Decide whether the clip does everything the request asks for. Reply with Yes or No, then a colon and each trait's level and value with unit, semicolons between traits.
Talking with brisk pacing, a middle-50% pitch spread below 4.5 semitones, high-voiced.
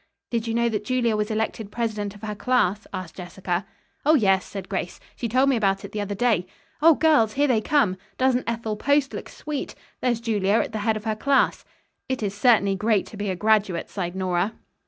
Yes: fast, 215 wpm; average, 3.4 semitones; high, 215 Hz